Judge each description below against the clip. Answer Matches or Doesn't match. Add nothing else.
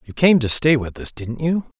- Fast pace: Matches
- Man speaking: Matches